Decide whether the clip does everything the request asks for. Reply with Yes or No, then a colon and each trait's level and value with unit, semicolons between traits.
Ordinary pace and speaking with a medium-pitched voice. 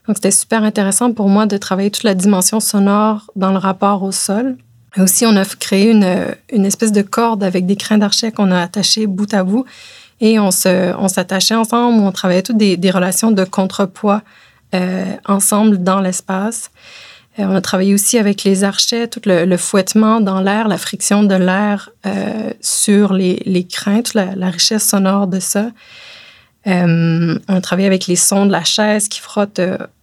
No: average, 195 wpm; high, 200 Hz